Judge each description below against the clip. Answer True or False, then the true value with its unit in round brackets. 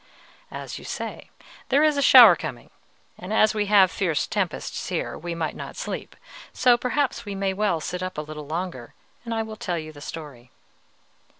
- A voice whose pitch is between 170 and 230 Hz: True (185 Hz)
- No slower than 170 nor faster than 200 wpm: True (195 wpm)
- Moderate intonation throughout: False (6.0 semitones)